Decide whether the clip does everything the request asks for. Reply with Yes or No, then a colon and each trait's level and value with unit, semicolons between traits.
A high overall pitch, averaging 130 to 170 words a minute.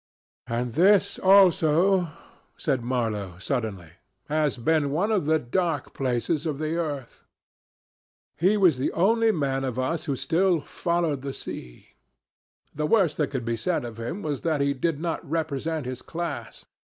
No: medium, 150 Hz; average, 155 wpm